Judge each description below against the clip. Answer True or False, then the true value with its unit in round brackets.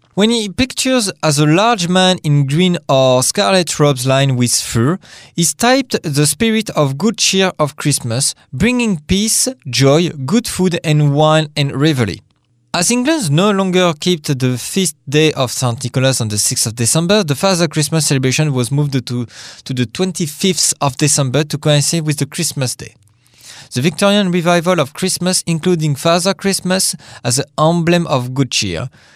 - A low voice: False (155 Hz)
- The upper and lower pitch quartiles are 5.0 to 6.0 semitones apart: True (5.5 semitones)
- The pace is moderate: True (165 wpm)